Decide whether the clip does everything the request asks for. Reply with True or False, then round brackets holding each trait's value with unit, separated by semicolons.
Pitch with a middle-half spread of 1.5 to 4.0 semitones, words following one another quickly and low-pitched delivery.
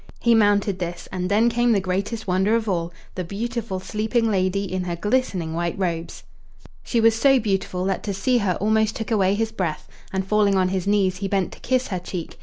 False (3.1 semitones; 210 wpm; 200 Hz)